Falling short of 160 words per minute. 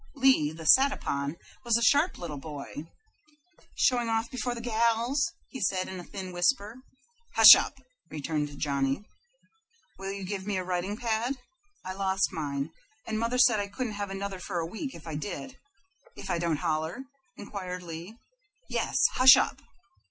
No: average, 165 wpm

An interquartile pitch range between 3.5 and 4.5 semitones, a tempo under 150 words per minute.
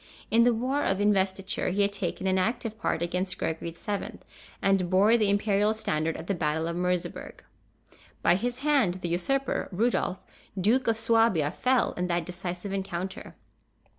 No: average, 4.0 semitones; average, 165 wpm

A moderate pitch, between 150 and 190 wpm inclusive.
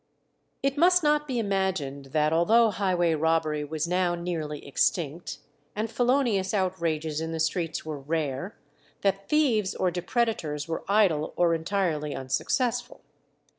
No: medium, 175 Hz; slow, 135 wpm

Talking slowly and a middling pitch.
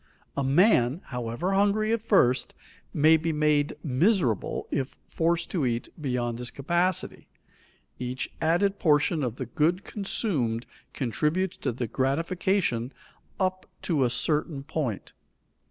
Yes: slow, 125 wpm; medium, 150 Hz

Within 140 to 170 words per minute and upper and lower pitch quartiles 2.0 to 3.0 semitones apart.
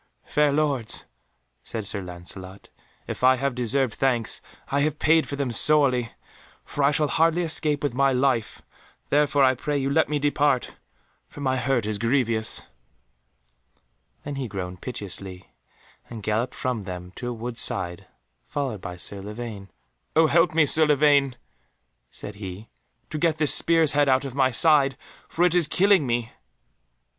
No: average, 160 wpm; average, 4.8 semitones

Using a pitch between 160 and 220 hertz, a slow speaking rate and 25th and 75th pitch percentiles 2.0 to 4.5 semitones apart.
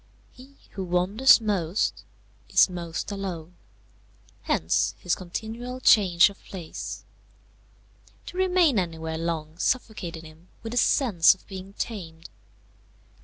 No: medium, 185 Hz; slow, 115 wpm; average, 5.0 semitones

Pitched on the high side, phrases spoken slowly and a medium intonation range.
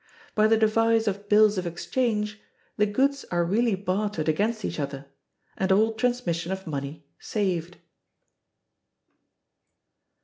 Yes: high, 205 Hz; slow, 125 wpm; average, 4.2 semitones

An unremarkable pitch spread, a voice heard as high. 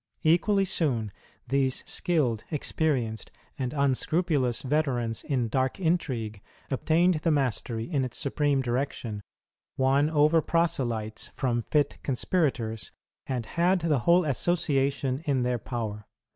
No: average, 4.7 semitones; low, 135 Hz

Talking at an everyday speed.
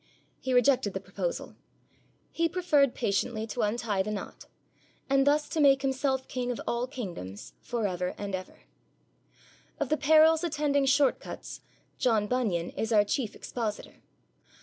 Yes: average, 150 wpm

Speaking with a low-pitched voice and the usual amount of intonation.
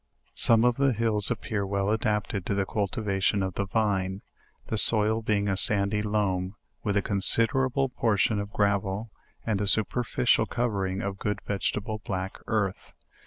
No: low, 105 Hz; narrow, 2.1 semitones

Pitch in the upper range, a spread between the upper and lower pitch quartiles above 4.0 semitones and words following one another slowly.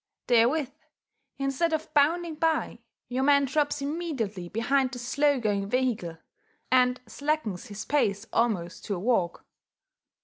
Yes: very high, 255 Hz; average, 5.1 semitones; slow, 130 wpm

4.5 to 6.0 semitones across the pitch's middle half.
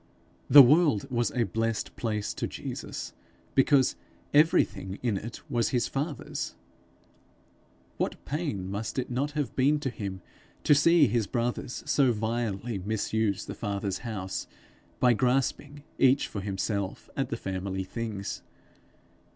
Yes: average, 5.0 semitones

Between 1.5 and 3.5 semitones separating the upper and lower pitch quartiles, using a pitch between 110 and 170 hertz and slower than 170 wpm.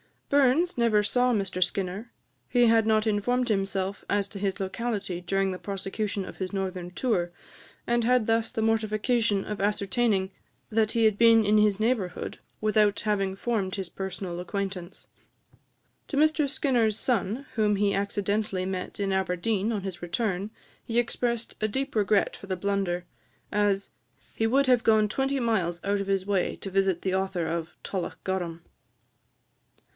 No: average, 3.0 semitones; high, 205 Hz; average, 160 wpm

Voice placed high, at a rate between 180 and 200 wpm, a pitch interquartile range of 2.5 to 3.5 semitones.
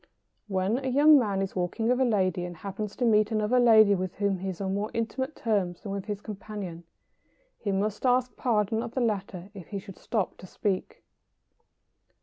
Yes: high, 205 Hz; average, 195 wpm; average, 3.1 semitones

